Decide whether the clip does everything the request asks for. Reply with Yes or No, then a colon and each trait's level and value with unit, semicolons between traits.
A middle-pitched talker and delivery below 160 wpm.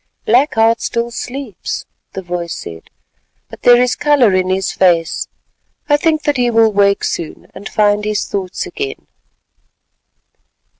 No: high, 220 Hz; average, 145 wpm